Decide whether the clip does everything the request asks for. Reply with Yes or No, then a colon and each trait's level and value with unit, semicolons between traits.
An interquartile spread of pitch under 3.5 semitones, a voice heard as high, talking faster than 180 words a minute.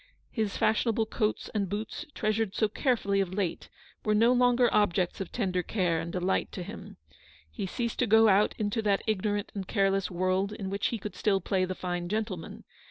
Yes: narrow, 2.6 semitones; high, 205 Hz; average, 195 wpm